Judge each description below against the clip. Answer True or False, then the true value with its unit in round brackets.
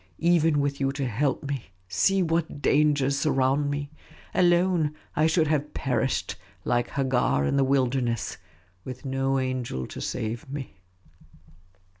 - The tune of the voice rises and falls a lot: False (2.6 semitones)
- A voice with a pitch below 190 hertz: True (135 Hz)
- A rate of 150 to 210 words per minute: False (135 wpm)